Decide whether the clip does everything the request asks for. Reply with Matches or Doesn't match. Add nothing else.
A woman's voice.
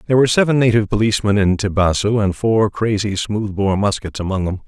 Doesn't match